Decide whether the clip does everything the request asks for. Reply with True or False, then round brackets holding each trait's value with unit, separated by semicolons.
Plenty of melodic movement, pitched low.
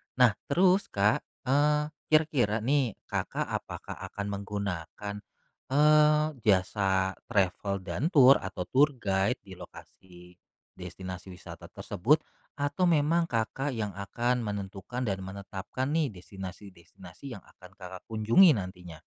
True (6.9 semitones; 105 Hz)